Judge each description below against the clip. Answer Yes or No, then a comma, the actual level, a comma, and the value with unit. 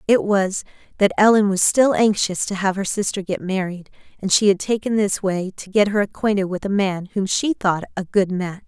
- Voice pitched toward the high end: Yes, high, 200 Hz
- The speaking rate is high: Yes, fast, 220 wpm